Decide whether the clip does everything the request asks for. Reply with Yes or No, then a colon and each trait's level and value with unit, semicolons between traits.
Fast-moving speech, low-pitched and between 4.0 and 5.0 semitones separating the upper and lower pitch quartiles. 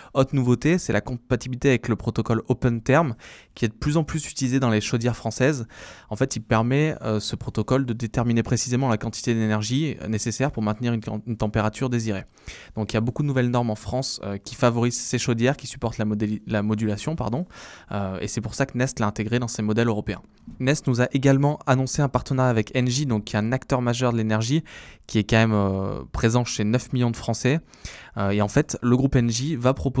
No: fast, 225 wpm; low, 120 Hz; average, 3.1 semitones